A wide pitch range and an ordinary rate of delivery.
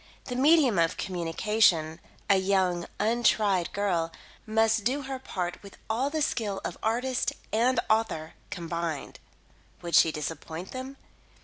No: wide, 5.9 semitones; slow, 130 wpm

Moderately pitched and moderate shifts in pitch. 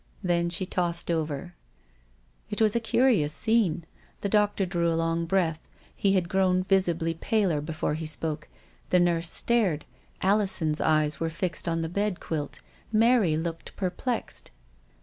Yes: medium, 175 Hz; average, 3.4 semitones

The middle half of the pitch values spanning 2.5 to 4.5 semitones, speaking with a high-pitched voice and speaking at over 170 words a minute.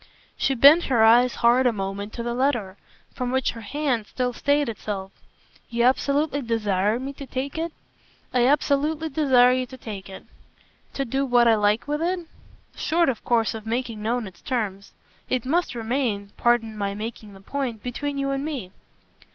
Yes: average, 4.0 semitones; high, 245 Hz; average, 180 wpm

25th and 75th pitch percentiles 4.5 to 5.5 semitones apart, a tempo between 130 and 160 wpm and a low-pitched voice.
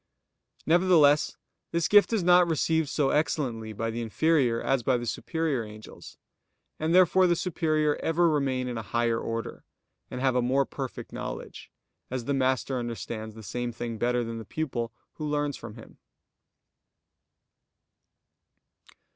Yes: average, 5.2 semitones; average, 145 wpm; low, 130 Hz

